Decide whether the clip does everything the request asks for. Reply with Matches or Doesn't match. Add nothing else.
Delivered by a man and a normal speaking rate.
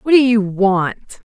Doesn't match